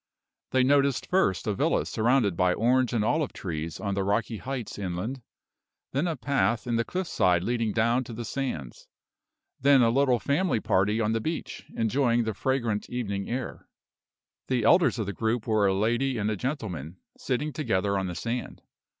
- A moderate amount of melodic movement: Yes, average, 4.5 semitones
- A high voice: No, low, 115 Hz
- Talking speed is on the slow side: No, average, 175 wpm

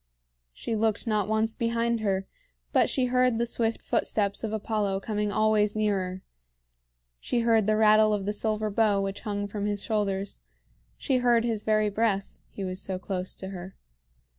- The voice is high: Yes, high, 210 Hz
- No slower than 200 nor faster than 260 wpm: No, average, 170 wpm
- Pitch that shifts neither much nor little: No, narrow, 2.1 semitones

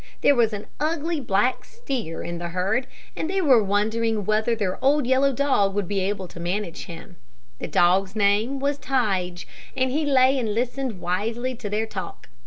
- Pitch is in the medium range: No, high, 220 Hz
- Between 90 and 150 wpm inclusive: No, average, 185 wpm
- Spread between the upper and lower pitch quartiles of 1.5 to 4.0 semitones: No, average, 5.2 semitones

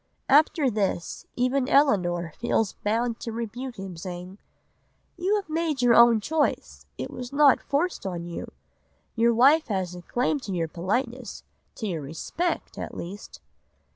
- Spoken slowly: No, average, 155 wpm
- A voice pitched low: No, high, 230 Hz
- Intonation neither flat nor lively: No, wide, 6.9 semitones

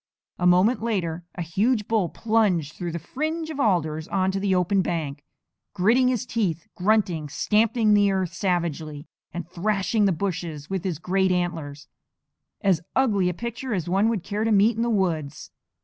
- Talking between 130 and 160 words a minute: No, average, 170 wpm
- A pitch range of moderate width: Yes, average, 4.2 semitones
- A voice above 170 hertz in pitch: Yes, high, 190 Hz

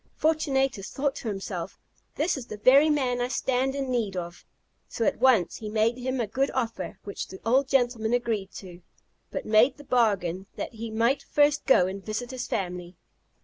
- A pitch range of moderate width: Yes, average, 4.8 semitones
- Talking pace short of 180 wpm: No, average, 190 wpm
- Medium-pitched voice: No, high, 235 Hz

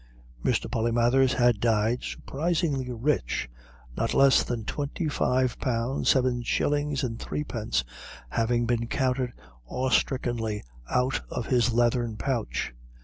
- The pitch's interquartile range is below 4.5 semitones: Yes, narrow, 2.4 semitones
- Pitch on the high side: No, low, 125 Hz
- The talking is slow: Yes, slow, 115 wpm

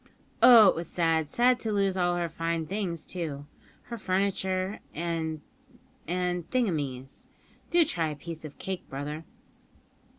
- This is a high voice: No, medium, 175 Hz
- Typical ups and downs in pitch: Yes, average, 3.5 semitones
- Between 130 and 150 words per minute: Yes, average, 140 wpm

